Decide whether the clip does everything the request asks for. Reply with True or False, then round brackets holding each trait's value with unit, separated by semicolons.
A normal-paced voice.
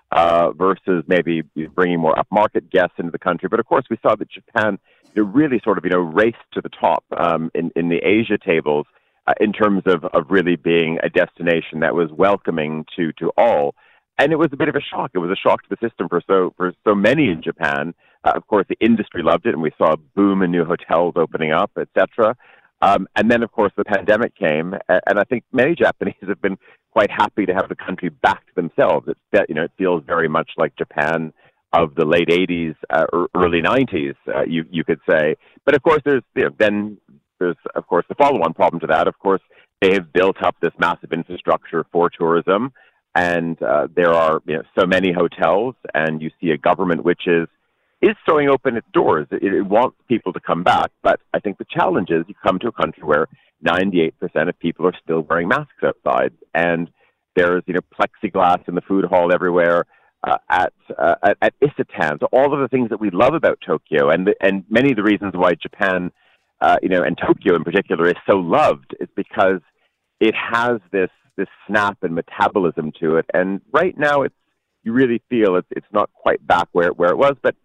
False (215 wpm)